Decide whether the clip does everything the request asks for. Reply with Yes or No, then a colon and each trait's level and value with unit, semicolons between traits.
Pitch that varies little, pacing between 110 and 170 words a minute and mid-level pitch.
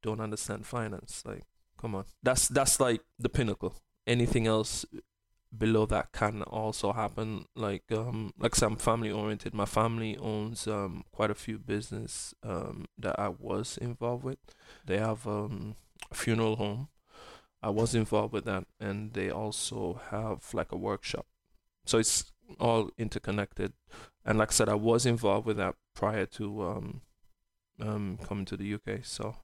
No: narrow, 1.7 semitones; average, 160 wpm; low, 110 Hz